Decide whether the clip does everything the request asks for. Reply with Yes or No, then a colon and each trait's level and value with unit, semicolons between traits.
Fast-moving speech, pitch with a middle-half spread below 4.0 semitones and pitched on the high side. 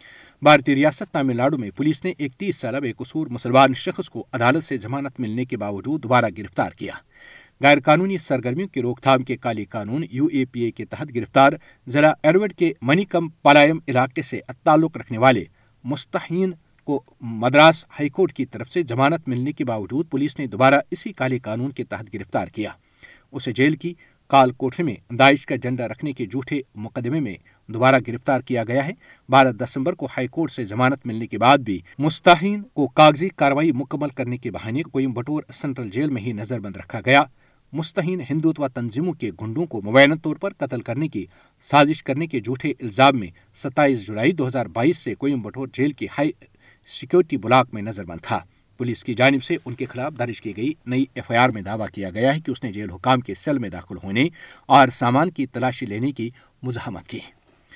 No: fast, 200 wpm; average, 3.6 semitones; low, 135 Hz